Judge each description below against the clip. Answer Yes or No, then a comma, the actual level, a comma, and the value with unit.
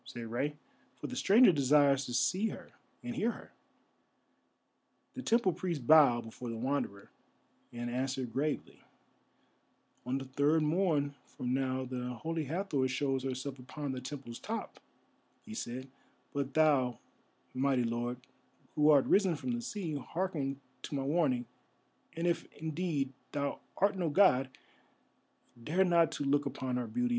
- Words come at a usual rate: Yes, average, 150 wpm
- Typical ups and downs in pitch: Yes, average, 4.4 semitones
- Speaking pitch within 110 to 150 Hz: Yes, medium, 140 Hz